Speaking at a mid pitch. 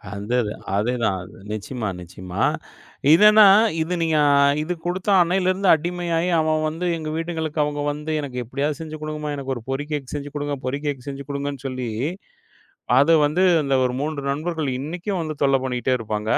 Yes: medium, 145 Hz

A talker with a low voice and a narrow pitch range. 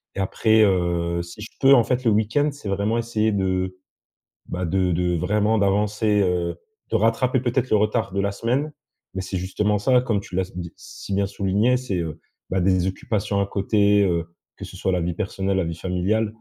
No: low, 100 Hz; average, 3.1 semitones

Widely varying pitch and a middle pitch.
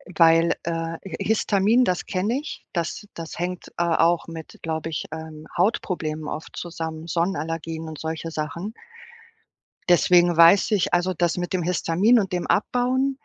No: average, 2.7 semitones; medium, 170 Hz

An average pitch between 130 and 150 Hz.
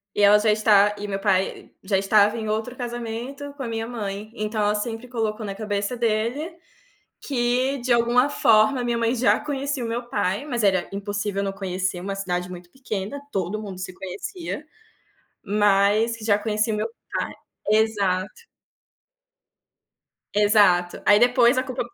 No: high, 215 Hz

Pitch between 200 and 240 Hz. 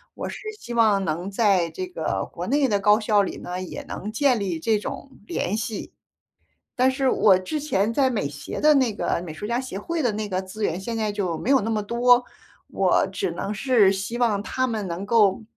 Yes: high, 215 Hz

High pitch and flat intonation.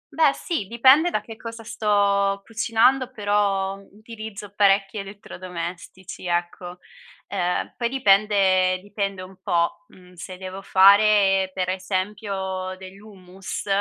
Yes: high, 195 Hz; narrow, 2.2 semitones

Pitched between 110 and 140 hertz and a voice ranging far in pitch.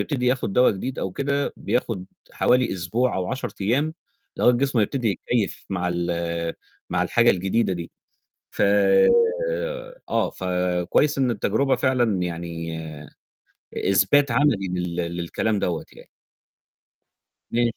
No: low, 100 Hz; wide, 6.1 semitones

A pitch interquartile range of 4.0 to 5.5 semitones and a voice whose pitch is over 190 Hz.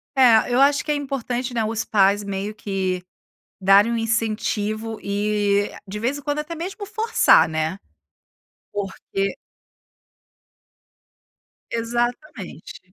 Yes: average, 4.6 semitones; high, 225 Hz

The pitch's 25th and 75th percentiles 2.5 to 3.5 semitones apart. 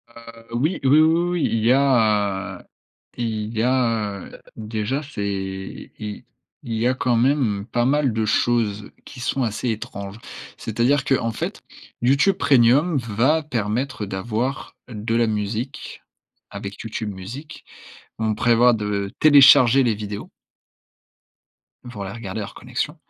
No: average, 3.9 semitones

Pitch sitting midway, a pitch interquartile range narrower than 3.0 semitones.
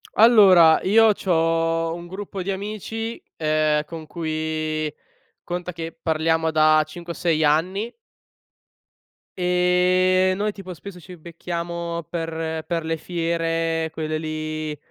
Yes: medium, 165 Hz; narrow, 2.4 semitones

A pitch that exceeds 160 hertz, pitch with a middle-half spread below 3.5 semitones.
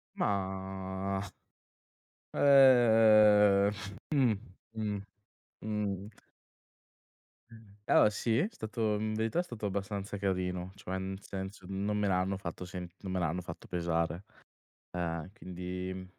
No: low, 100 Hz; narrow, 2.4 semitones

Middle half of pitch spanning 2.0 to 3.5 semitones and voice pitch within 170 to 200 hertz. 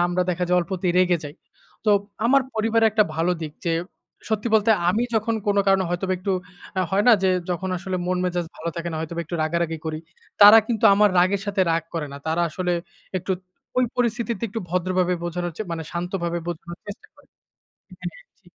Yes: average, 3.2 semitones; medium, 185 Hz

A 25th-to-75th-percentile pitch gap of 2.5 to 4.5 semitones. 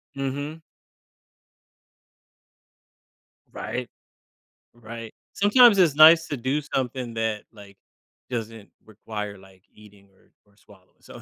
No: wide, 5.5 semitones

